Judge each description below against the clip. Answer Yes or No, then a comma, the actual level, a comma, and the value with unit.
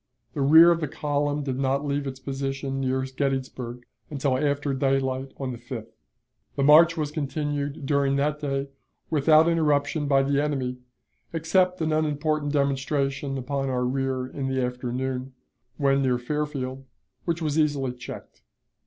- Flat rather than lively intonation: Yes, narrow, 2.0 semitones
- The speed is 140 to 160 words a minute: Yes, average, 150 wpm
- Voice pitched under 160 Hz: Yes, medium, 140 Hz